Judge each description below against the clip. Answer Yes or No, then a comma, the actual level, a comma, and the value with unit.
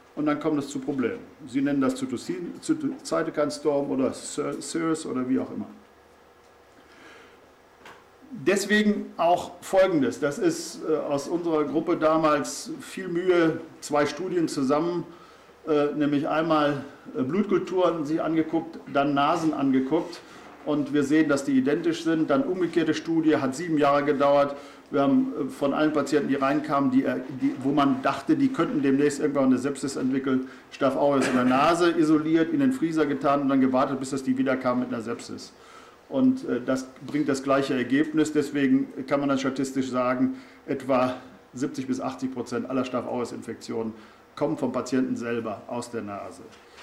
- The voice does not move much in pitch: No, average, 3.5 semitones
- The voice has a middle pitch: Yes, medium, 145 Hz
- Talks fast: No, average, 150 wpm